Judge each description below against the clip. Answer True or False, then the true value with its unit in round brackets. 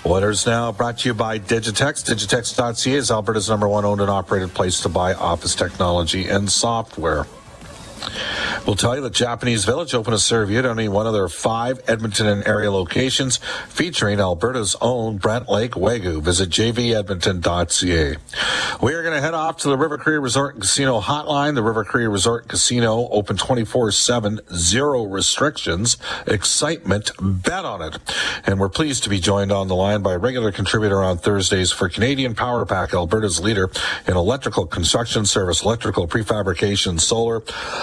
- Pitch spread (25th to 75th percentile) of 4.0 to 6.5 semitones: False (3.4 semitones)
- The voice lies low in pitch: True (110 Hz)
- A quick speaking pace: False (170 wpm)